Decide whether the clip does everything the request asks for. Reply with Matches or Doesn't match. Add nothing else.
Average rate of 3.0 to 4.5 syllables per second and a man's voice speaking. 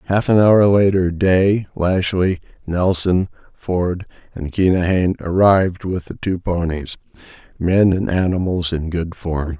Matches